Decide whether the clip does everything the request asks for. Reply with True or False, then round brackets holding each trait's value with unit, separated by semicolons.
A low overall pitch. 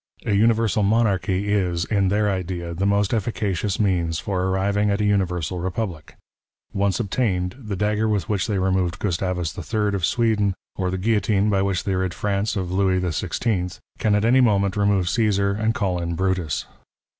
True (100 Hz)